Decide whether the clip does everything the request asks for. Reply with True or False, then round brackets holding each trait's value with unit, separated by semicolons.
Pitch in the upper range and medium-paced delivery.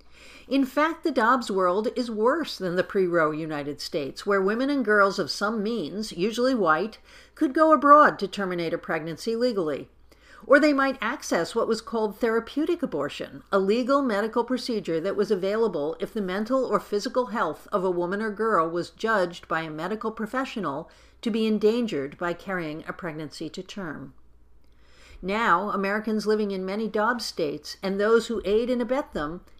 True (210 Hz; 170 wpm)